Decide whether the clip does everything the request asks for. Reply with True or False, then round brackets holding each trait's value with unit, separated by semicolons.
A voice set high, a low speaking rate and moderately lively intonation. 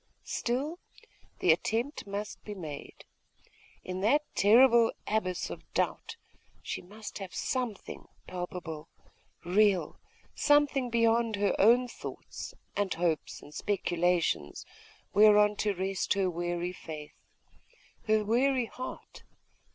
True (205 Hz; 110 wpm; 4.6 semitones)